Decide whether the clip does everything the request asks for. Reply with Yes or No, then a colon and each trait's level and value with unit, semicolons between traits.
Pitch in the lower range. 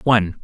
Yes: low, 105 Hz